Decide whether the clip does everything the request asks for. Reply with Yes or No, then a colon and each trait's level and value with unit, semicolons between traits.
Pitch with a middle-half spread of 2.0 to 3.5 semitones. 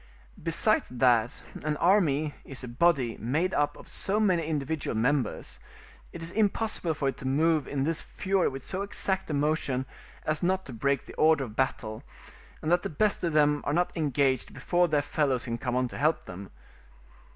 No: average, 4.4 semitones